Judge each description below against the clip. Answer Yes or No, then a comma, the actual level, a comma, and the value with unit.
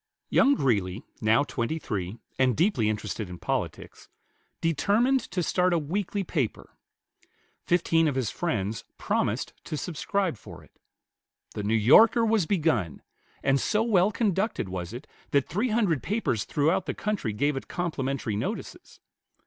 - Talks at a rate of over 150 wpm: No, average, 145 wpm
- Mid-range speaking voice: Yes, medium, 155 Hz